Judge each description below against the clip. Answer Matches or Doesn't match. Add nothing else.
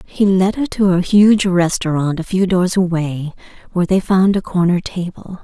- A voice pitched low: Doesn't match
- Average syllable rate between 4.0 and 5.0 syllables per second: Matches